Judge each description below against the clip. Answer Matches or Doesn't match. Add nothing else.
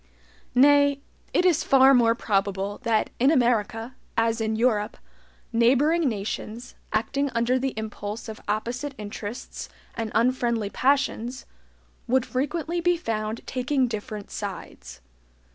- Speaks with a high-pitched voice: Matches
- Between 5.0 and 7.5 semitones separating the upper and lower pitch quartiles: Doesn't match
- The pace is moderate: Doesn't match